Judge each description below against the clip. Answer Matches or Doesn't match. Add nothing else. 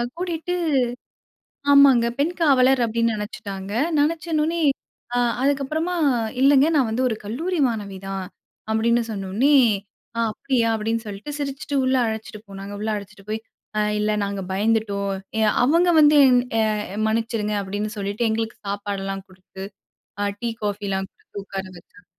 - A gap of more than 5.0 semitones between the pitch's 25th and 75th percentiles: Matches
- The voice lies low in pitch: Doesn't match